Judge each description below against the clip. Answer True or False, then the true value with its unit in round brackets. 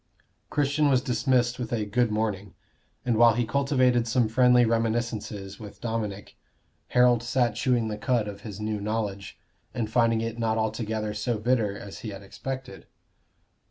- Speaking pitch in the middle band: False (115 Hz)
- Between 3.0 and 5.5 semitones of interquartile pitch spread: False (2.5 semitones)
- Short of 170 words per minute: True (160 wpm)